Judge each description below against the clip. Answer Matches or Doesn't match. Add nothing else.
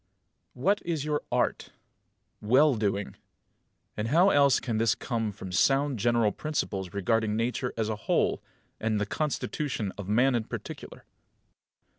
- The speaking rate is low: Doesn't match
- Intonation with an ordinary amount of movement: Matches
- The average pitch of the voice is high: Doesn't match